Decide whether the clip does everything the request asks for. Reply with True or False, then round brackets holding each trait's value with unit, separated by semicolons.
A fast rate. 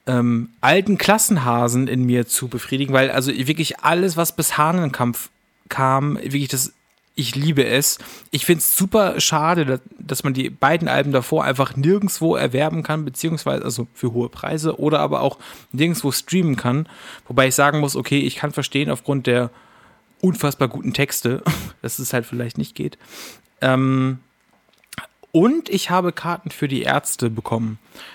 False (160 wpm)